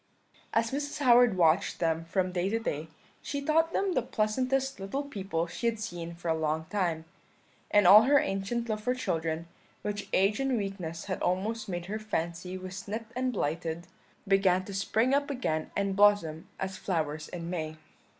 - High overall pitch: Yes, high, 195 Hz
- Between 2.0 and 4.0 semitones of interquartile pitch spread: No, average, 5.3 semitones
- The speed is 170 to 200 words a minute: Yes, average, 180 wpm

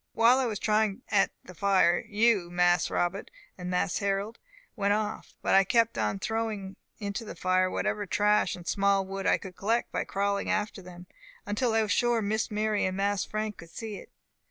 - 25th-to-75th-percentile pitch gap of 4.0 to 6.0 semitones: No, narrow, 2.5 semitones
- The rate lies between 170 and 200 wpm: Yes, average, 195 wpm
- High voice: Yes, high, 200 Hz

